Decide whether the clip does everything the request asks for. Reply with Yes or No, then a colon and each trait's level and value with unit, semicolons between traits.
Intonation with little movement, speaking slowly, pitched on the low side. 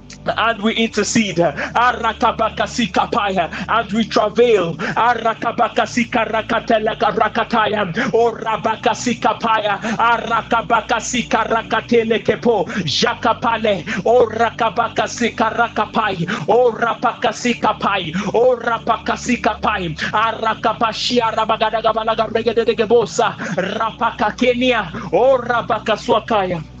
No: narrow, 1.2 semitones; slow, 65 wpm; high, 225 Hz